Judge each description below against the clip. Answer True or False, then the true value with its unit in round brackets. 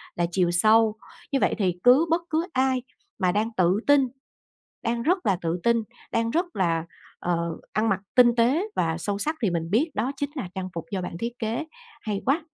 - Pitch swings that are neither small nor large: False (6.3 semitones)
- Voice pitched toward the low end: False (220 Hz)